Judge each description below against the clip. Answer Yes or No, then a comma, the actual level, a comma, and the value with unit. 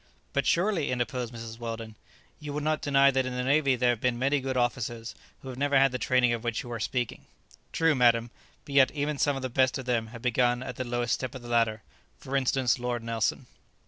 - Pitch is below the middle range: Yes, low, 125 Hz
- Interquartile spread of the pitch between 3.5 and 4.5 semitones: No, narrow, 2.4 semitones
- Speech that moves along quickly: Yes, fast, 235 wpm